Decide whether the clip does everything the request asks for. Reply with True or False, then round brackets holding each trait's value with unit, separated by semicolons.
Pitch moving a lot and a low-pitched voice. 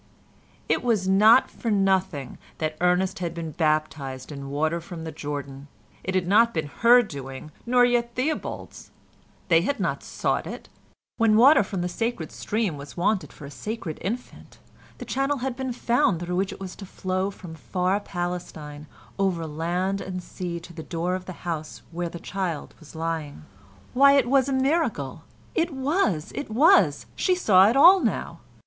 False (6.3 semitones; 185 Hz)